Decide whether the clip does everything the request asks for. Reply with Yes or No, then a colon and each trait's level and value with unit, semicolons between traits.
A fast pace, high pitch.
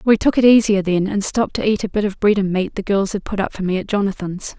Yes: fast, 315 wpm; high, 200 Hz